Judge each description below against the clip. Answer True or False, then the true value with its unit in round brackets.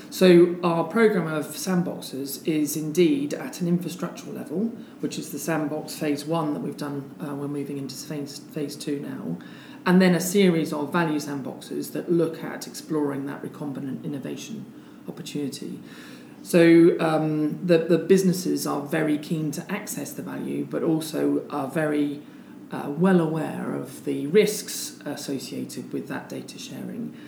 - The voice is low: False (155 Hz)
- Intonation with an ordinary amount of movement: True (3.4 semitones)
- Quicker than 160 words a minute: False (155 wpm)